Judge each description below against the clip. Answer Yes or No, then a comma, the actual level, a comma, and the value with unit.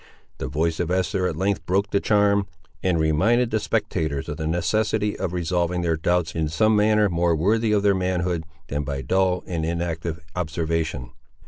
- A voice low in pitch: Yes, very low, 90 Hz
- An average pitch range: Yes, average, 3.7 semitones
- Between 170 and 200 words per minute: Yes, average, 180 wpm